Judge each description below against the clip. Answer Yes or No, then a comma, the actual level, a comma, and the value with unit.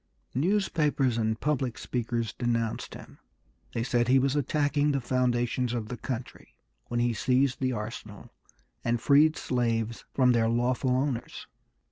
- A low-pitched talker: Yes, low, 125 Hz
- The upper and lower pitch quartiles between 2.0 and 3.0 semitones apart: Yes, narrow, 2.6 semitones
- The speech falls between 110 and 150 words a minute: Yes, average, 140 wpm